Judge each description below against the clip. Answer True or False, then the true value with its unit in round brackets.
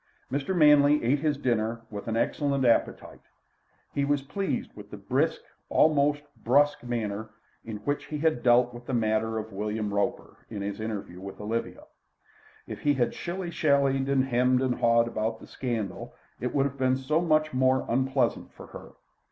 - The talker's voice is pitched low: True (130 Hz)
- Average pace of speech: True (175 wpm)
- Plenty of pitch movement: False (4.2 semitones)